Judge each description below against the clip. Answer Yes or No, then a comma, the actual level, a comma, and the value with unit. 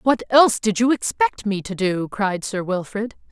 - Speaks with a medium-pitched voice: No, high, 215 Hz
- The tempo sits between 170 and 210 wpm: Yes, average, 200 wpm